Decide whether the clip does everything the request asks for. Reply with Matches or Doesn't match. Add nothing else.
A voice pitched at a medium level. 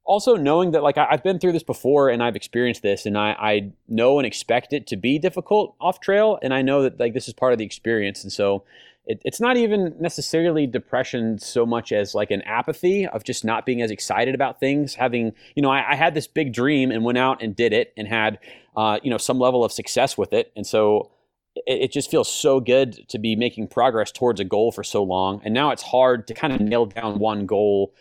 Doesn't match